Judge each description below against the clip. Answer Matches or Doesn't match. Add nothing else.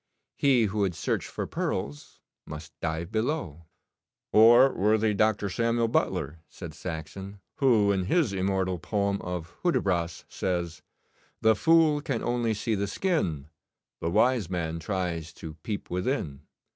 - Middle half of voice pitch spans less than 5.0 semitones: Doesn't match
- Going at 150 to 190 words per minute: Doesn't match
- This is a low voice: Matches